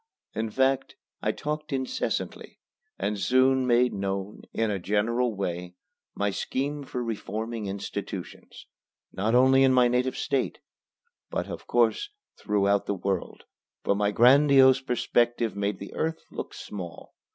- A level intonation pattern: No, average, 4.5 semitones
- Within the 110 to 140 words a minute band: Yes, slow, 135 wpm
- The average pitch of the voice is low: Yes, low, 120 Hz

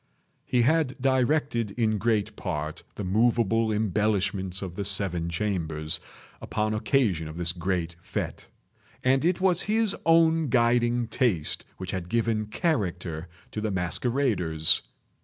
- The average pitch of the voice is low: Yes, low, 105 Hz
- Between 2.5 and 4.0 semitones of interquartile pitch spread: No, wide, 5.4 semitones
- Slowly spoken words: Yes, slow, 130 wpm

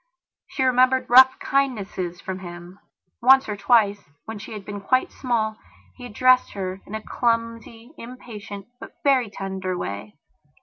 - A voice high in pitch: Yes, high, 220 Hz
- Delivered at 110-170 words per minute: Yes, average, 150 wpm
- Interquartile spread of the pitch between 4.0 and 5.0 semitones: Yes, average, 4.6 semitones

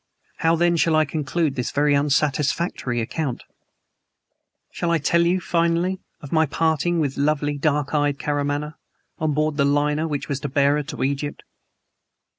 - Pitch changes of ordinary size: No, narrow, 2.3 semitones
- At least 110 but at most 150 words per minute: No, average, 160 wpm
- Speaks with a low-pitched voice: No, medium, 150 Hz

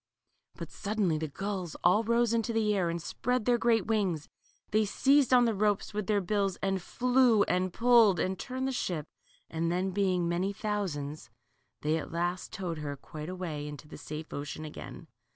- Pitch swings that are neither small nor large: Yes, average, 4.7 semitones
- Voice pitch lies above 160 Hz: Yes, high, 190 Hz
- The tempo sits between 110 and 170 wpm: No, average, 185 wpm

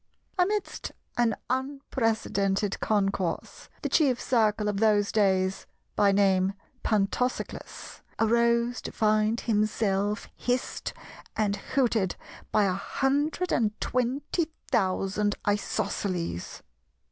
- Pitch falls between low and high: No, high, 215 Hz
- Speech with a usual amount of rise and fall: Yes, average, 3.6 semitones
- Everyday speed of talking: No, slow, 90 wpm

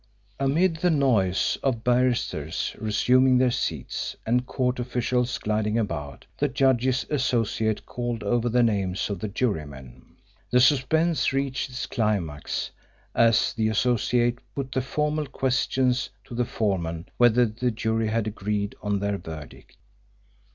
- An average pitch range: Yes, average, 3.6 semitones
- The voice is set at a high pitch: No, low, 120 Hz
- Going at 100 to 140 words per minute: Yes, slow, 135 wpm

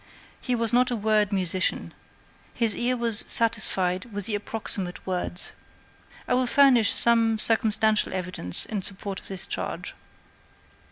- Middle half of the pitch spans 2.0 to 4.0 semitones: Yes, average, 3.3 semitones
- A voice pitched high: Yes, high, 215 Hz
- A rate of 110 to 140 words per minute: Yes, slow, 135 wpm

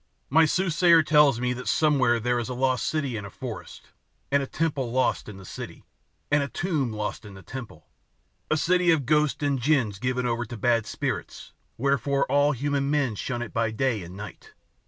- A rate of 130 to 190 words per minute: No, average, 200 wpm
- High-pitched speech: No, low, 130 Hz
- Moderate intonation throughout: Yes, average, 4.0 semitones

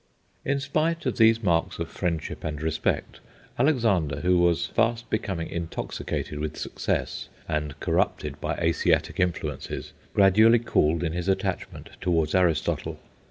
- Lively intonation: Yes, wide, 5.9 semitones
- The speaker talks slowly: Yes, slow, 130 wpm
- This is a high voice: No, very low, 90 Hz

